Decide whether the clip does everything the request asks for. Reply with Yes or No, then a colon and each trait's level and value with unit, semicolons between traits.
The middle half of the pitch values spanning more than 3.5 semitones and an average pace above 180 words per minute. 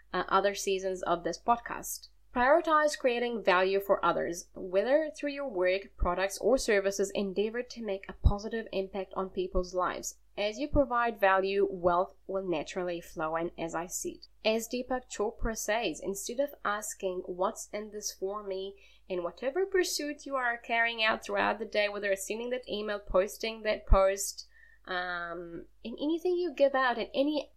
No: average, 4.8 semitones; average, 170 wpm